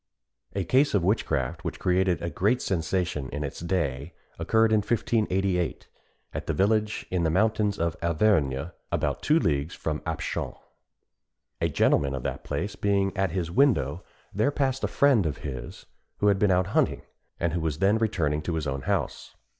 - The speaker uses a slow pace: No, average, 175 wpm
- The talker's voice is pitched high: No, very low, 90 Hz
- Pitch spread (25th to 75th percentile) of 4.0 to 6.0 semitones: Yes, average, 5.0 semitones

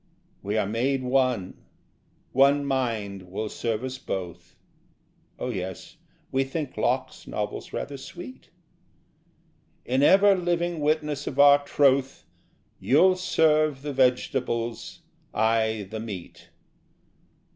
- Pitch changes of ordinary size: Yes, average, 4.6 semitones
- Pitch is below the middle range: Yes, low, 130 Hz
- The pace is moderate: No, slow, 110 wpm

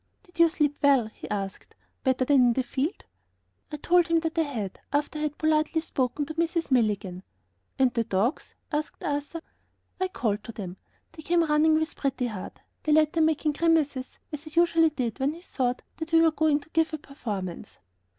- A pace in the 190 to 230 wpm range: Yes, average, 200 wpm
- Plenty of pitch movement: No, average, 4.3 semitones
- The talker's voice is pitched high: Yes, very high, 295 Hz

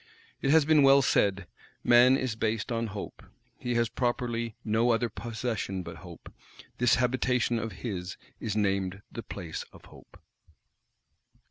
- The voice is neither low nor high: No, low, 115 Hz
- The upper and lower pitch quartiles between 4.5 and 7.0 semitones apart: No, average, 3.2 semitones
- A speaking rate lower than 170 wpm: Yes, average, 145 wpm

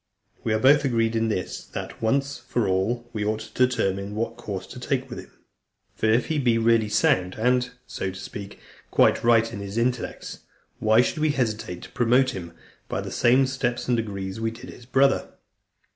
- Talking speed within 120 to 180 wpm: No, average, 195 wpm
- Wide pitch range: No, average, 2.9 semitones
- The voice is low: Yes, low, 115 Hz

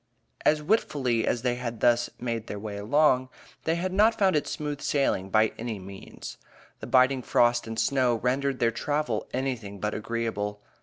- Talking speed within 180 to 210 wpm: No, average, 170 wpm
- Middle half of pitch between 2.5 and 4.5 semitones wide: Yes, average, 4.0 semitones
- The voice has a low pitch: Yes, low, 120 Hz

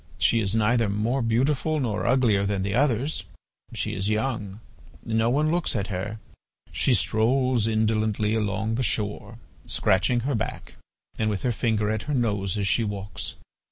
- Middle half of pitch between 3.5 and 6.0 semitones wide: No, average, 3.1 semitones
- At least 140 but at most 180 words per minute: Yes, average, 160 wpm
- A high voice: No, low, 110 Hz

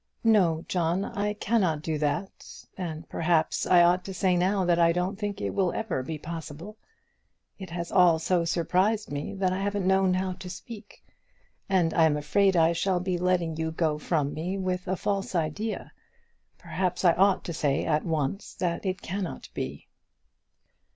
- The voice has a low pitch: No, medium, 180 Hz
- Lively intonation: No, average, 2.8 semitones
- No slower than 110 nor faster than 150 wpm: No, average, 180 wpm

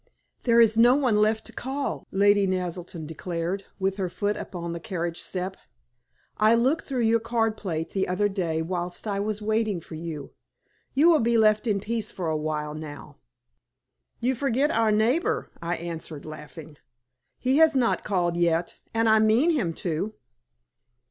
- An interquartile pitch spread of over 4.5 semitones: Yes, average, 5.1 semitones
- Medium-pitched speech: No, high, 200 Hz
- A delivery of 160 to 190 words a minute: Yes, average, 170 wpm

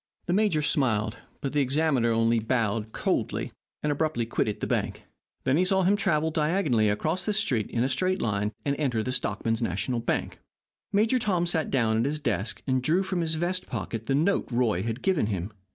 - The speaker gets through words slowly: No, average, 195 wpm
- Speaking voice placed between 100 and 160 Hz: Yes, low, 135 Hz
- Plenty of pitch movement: Yes, wide, 7.0 semitones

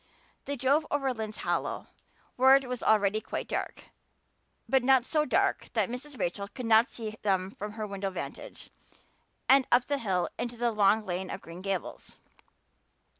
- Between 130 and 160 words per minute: No, average, 175 wpm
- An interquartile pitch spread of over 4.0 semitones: Yes, average, 4.7 semitones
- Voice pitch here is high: Yes, high, 225 Hz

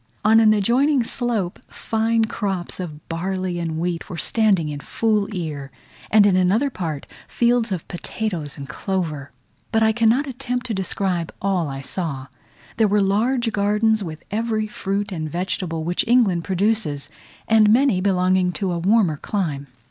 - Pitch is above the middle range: Yes, high, 195 Hz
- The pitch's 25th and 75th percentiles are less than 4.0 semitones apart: No, average, 4.5 semitones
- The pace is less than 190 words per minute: Yes, average, 155 wpm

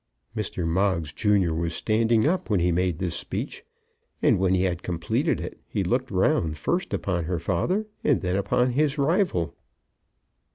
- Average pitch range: No, wide, 5.7 semitones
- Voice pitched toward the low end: Yes, very low, 95 Hz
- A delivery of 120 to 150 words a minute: No, average, 165 wpm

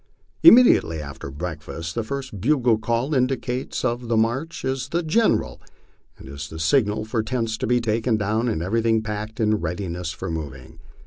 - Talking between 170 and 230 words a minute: Yes, average, 175 wpm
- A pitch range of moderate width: No, wide, 5.9 semitones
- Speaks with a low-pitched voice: Yes, low, 110 Hz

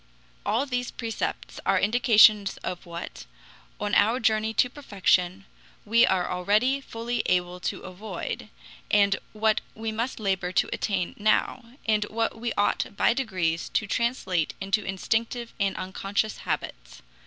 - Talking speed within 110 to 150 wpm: Yes, average, 140 wpm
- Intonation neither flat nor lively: Yes, average, 3.4 semitones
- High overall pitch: Yes, high, 210 Hz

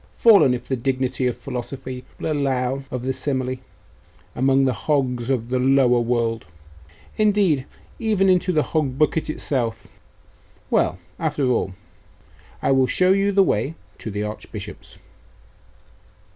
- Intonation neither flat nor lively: Yes, average, 3.6 semitones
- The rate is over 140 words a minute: No, slow, 135 wpm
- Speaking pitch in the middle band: No, low, 130 Hz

